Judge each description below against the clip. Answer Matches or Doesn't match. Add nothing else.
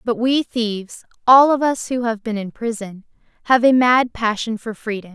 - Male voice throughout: Doesn't match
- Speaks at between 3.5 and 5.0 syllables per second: Matches